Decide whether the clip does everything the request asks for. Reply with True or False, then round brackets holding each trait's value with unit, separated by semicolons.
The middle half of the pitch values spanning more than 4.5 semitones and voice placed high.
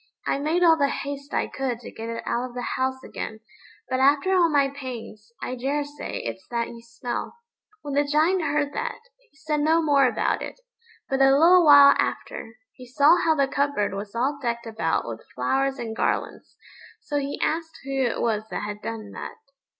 False (3.9 semitones; 275 Hz)